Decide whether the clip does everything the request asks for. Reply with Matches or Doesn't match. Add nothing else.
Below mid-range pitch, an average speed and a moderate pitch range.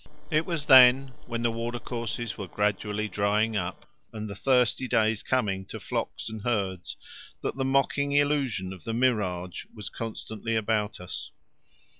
Matches